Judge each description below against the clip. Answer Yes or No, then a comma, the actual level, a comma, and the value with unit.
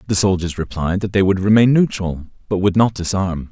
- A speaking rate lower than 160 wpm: No, fast, 205 wpm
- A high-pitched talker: No, very low, 95 Hz